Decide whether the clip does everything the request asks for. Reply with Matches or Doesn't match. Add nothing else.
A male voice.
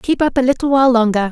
Doesn't match